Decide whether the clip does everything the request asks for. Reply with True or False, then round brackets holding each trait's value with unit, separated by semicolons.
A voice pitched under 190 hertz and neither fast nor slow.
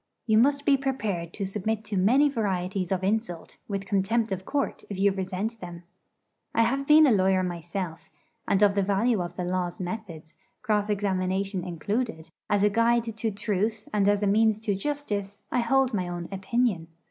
False (200 Hz; 180 wpm)